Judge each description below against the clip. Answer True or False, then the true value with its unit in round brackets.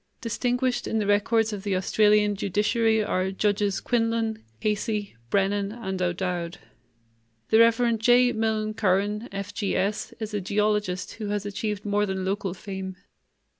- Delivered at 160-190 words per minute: False (135 wpm)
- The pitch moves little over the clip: True (2.1 semitones)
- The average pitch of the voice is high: True (210 Hz)